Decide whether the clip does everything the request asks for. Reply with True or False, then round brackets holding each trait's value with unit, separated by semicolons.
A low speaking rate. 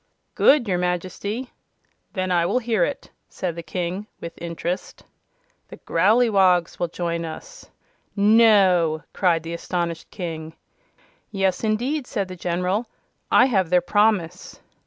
True (130 wpm)